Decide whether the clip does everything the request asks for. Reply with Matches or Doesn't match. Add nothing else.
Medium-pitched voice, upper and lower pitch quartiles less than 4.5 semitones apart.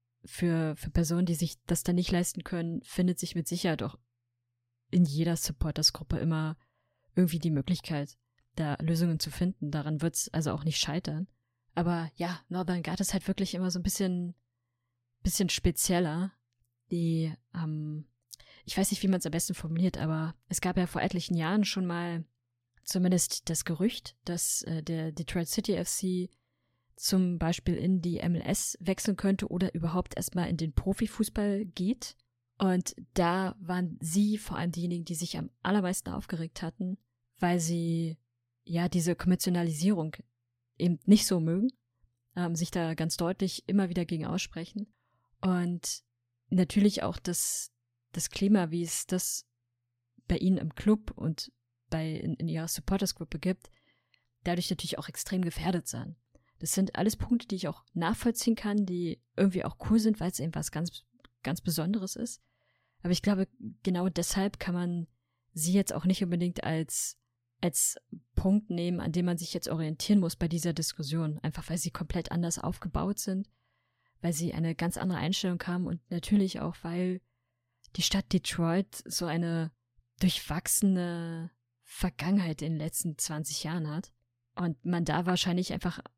Matches